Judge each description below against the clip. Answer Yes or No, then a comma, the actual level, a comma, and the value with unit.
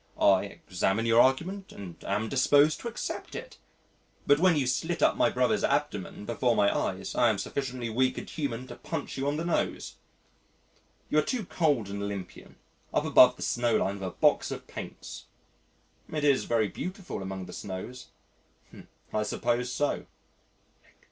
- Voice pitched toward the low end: Yes, low, 125 Hz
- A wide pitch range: Yes, wide, 6.2 semitones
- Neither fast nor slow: Yes, average, 165 wpm